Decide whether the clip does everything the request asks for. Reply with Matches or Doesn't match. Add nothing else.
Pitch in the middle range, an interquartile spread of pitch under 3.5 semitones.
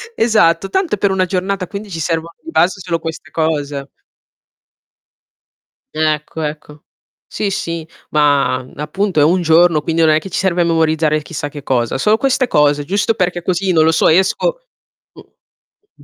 Doesn't match